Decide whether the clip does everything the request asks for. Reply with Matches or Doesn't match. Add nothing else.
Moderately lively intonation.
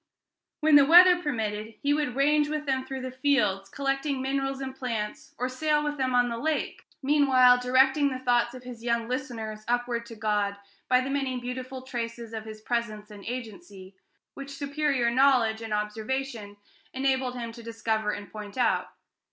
Matches